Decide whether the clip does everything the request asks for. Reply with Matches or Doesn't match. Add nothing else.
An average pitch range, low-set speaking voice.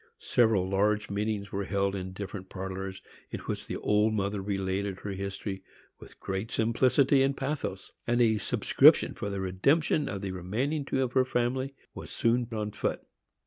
Matches